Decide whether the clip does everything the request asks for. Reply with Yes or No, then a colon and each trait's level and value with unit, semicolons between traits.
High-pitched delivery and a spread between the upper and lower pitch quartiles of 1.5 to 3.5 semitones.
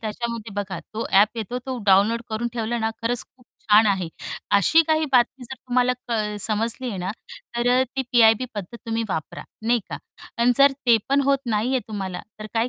Yes: high, 230 Hz; average, 2.8 semitones